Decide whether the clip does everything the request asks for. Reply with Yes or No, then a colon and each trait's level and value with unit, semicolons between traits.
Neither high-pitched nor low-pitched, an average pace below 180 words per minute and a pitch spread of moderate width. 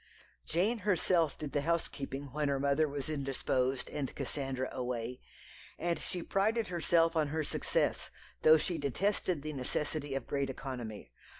Yes: medium, 145 Hz; average, 145 wpm; average, 3.7 semitones